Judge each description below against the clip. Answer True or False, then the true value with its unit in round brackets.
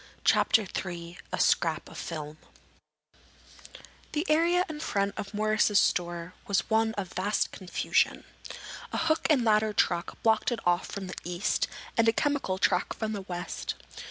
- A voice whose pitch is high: True (205 Hz)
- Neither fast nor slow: True (155 wpm)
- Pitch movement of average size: True (4.2 semitones)